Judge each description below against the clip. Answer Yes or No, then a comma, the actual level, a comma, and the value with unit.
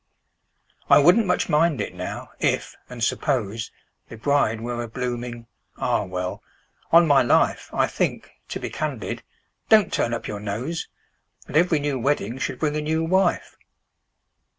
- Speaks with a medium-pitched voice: No, low, 130 Hz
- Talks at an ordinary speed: No, slow, 130 wpm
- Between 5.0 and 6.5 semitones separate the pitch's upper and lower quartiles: Yes, wide, 5.6 semitones